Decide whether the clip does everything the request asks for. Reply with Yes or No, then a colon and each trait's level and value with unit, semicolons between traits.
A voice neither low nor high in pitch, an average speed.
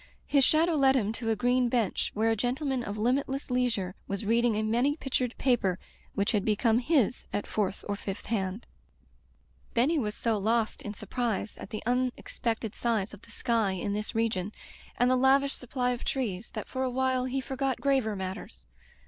No: high, 235 Hz; average, 185 wpm